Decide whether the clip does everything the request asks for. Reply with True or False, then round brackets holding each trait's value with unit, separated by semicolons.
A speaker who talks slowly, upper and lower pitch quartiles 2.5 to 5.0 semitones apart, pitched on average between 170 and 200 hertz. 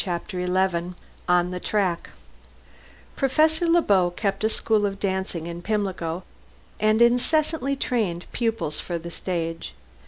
True (130 wpm; 4.5 semitones; 190 Hz)